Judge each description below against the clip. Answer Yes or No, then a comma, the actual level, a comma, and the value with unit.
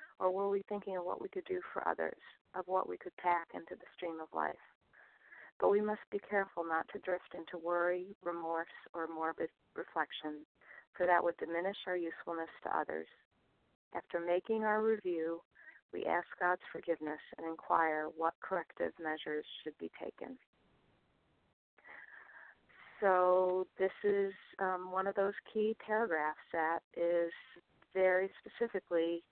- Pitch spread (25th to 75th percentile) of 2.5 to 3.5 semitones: Yes, average, 2.9 semitones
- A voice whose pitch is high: No, medium, 180 Hz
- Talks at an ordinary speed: Yes, average, 145 wpm